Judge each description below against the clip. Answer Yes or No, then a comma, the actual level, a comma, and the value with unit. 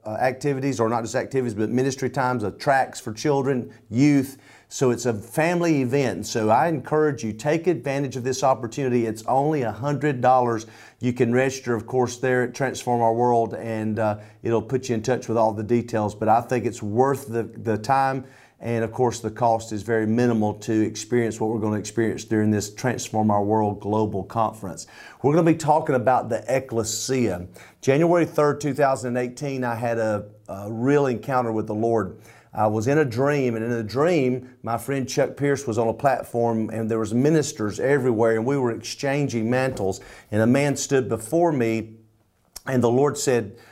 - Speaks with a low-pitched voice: Yes, low, 120 Hz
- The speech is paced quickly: No, average, 190 wpm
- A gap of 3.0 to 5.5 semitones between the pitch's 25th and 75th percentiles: Yes, average, 3.3 semitones